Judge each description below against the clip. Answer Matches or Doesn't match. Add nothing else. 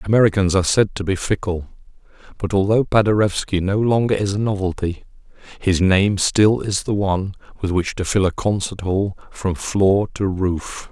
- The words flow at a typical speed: Matches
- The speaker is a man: Matches